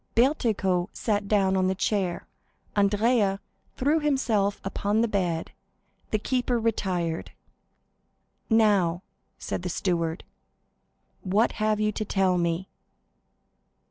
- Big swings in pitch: No, average, 3.2 semitones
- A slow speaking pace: Yes, slow, 110 wpm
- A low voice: No, high, 200 Hz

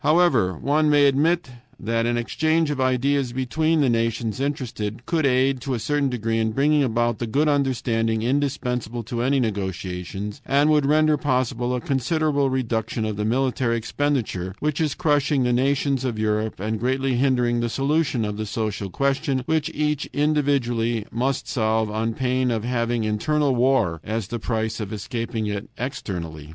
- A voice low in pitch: Yes, low, 125 Hz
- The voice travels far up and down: No, average, 3.9 semitones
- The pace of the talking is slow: No, average, 165 wpm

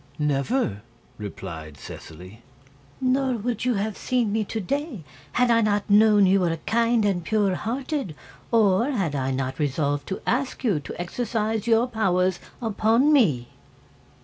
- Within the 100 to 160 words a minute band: Yes, average, 150 wpm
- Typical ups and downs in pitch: No, wide, 7.2 semitones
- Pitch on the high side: Yes, high, 210 Hz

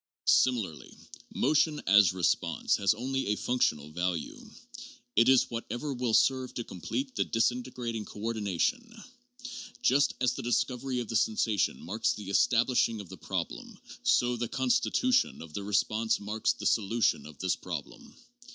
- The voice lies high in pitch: No, low, 115 Hz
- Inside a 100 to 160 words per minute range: Yes, average, 150 wpm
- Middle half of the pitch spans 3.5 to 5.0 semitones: Yes, average, 4.0 semitones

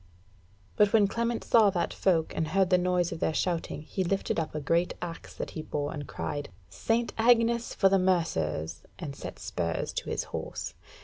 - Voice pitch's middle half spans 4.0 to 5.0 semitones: Yes, average, 4.5 semitones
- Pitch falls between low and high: Yes, medium, 175 Hz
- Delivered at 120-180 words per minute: No, average, 190 wpm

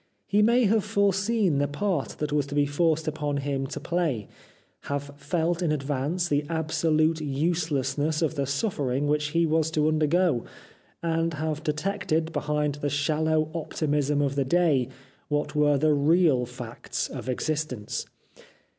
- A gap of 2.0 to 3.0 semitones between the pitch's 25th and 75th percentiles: Yes, narrow, 2.4 semitones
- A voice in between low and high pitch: Yes, medium, 150 Hz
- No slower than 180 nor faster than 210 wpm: No, average, 150 wpm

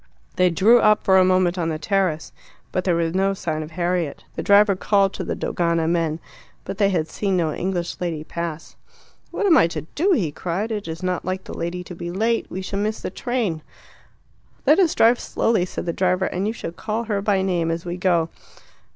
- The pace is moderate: No, fast, 220 wpm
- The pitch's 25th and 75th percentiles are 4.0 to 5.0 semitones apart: No, average, 3.2 semitones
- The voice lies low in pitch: No, medium, 185 Hz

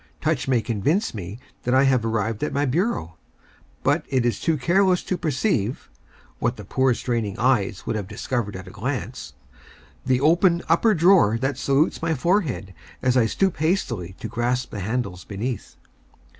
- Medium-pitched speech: No, low, 125 Hz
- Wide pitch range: Yes, wide, 6.3 semitones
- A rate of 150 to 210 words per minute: Yes, average, 170 wpm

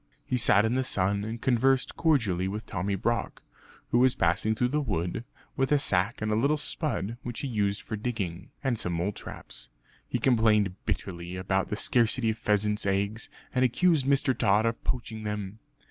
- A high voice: No, low, 110 Hz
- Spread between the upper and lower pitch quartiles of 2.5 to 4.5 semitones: Yes, average, 3.9 semitones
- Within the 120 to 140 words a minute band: No, average, 185 wpm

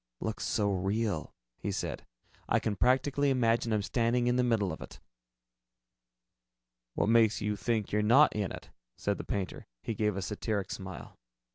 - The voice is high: No, low, 110 Hz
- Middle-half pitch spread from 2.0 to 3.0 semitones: Yes, average, 2.7 semitones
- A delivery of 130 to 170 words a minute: Yes, average, 165 wpm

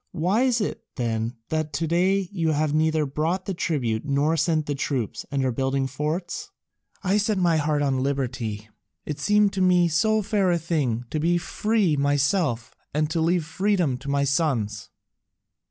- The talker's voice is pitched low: No, medium, 155 Hz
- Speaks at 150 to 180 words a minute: Yes, average, 175 wpm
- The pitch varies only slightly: No, average, 4.6 semitones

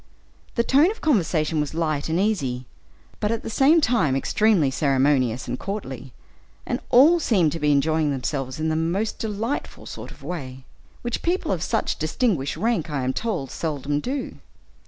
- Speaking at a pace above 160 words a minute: Yes, average, 175 wpm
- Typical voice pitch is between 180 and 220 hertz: No, medium, 160 Hz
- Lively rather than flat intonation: Yes, wide, 8.0 semitones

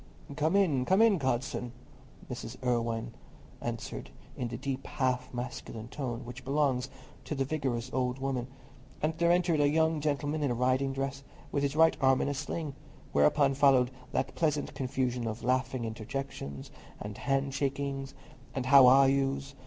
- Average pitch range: No, narrow, 2.3 semitones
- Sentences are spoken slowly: No, average, 160 wpm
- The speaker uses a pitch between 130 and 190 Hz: Yes, low, 135 Hz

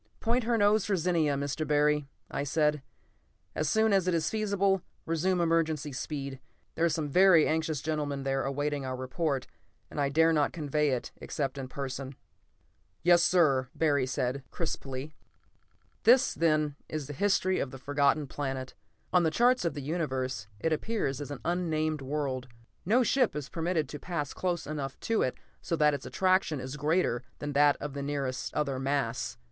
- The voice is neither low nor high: Yes, medium, 150 Hz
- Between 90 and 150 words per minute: No, average, 175 wpm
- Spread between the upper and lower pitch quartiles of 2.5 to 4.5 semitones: Yes, average, 3.6 semitones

